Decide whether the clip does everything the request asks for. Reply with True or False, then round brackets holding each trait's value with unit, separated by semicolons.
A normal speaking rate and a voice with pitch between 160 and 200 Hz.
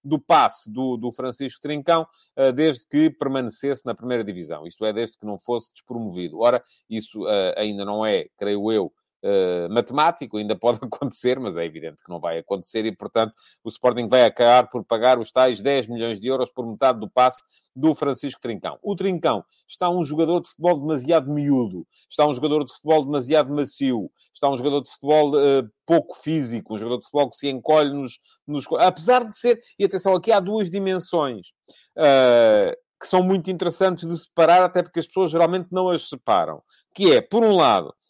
False (190 wpm; 140 Hz)